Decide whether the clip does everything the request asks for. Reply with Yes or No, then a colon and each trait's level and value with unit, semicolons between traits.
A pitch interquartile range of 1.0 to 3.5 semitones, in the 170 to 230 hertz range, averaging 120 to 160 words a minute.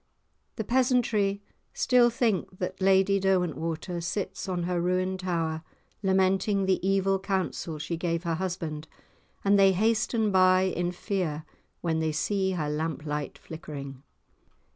Yes: average, 2.9 semitones; medium, 185 Hz; slow, 135 wpm